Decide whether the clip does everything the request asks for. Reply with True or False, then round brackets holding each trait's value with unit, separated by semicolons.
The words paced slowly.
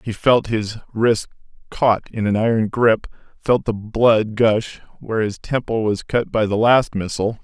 False (180 wpm)